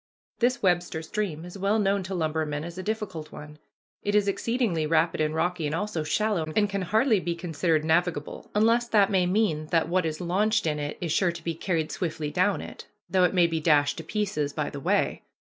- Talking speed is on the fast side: Yes, fast, 215 wpm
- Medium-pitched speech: Yes, medium, 175 Hz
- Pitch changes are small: No, average, 4.2 semitones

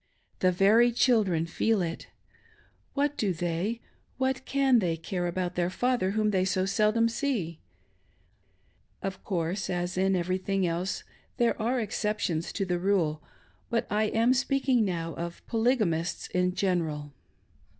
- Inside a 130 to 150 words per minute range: Yes, average, 140 wpm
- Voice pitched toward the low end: No, high, 190 Hz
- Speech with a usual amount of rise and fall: Yes, average, 4.5 semitones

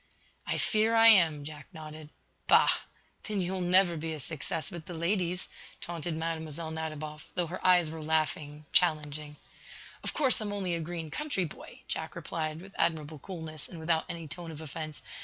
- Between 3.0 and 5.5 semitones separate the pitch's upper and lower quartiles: No, narrow, 2.5 semitones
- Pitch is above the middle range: No, medium, 160 Hz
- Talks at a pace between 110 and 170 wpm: No, average, 180 wpm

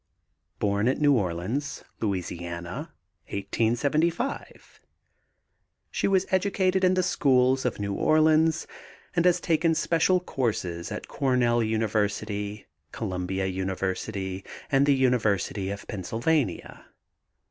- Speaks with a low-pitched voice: Yes, low, 115 Hz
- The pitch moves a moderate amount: No, wide, 7.8 semitones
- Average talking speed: No, slow, 105 wpm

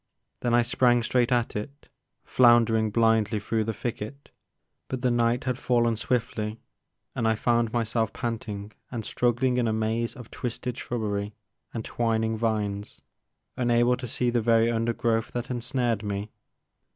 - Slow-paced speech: No, average, 150 wpm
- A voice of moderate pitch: No, low, 115 Hz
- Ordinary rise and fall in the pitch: No, narrow, 1.6 semitones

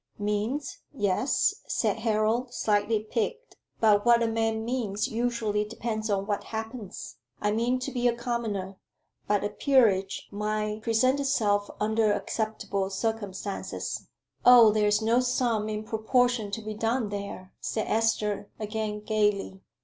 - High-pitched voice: Yes, high, 220 Hz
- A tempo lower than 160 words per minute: Yes, average, 140 wpm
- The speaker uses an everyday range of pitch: No, narrow, 2.2 semitones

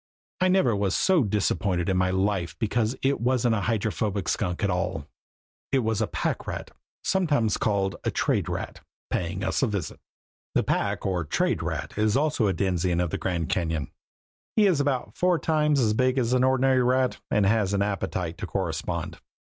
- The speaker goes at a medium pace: Yes, average, 185 wpm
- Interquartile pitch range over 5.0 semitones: Yes, wide, 5.5 semitones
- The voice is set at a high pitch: No, low, 110 Hz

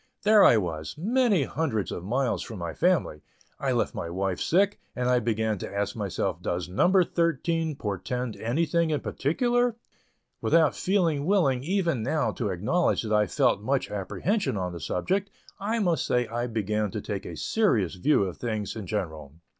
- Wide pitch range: Yes, wide, 9.0 semitones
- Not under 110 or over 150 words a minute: No, average, 175 wpm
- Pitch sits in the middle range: No, low, 125 Hz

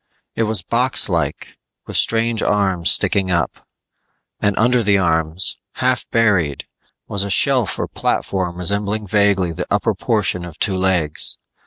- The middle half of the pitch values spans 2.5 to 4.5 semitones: Yes, average, 3.6 semitones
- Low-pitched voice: Yes, low, 100 Hz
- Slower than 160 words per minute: Yes, average, 140 wpm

